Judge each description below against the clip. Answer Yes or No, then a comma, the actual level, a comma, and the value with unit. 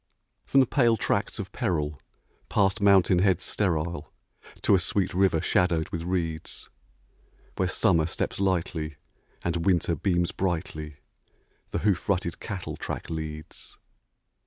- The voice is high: No, very low, 90 Hz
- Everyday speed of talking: No, slow, 130 wpm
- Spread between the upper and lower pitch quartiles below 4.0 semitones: Yes, average, 3.2 semitones